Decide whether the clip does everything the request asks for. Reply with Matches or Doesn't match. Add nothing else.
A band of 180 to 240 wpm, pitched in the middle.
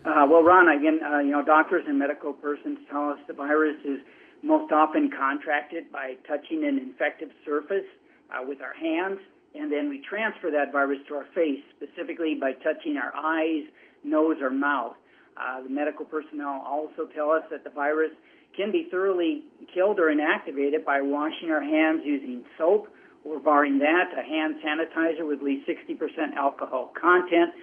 Doesn't match